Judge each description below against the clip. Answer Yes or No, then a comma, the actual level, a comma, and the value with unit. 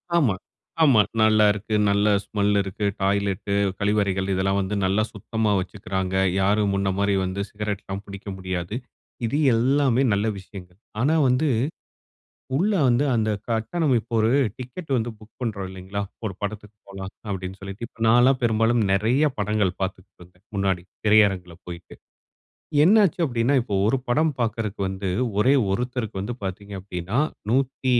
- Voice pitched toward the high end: No, low, 105 Hz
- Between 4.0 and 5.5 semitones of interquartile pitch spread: No, average, 3.4 semitones